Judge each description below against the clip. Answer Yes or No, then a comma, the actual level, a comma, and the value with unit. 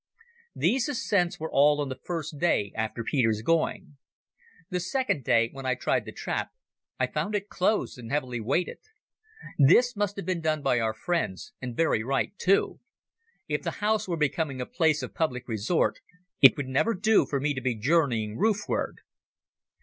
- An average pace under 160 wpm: No, average, 180 wpm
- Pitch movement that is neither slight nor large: No, wide, 6.2 semitones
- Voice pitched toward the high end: No, medium, 150 Hz